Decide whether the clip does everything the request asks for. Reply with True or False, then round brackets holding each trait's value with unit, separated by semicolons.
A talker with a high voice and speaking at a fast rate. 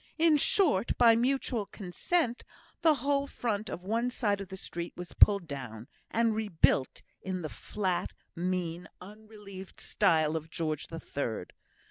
False (195 Hz; 145 wpm)